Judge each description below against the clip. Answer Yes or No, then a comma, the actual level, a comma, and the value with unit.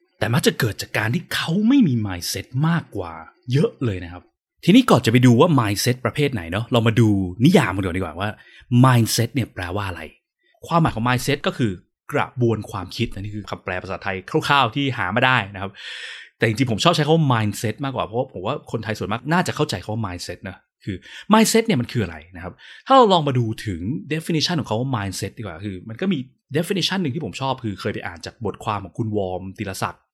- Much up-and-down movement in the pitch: Yes, wide, 6.0 semitones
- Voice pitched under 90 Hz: No, low, 115 Hz